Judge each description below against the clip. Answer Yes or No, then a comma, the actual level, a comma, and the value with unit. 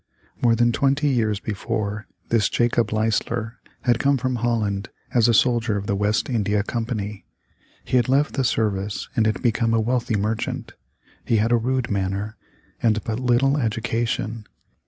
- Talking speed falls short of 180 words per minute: Yes, average, 160 wpm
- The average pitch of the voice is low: Yes, low, 115 Hz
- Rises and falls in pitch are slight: Yes, narrow, 2.2 semitones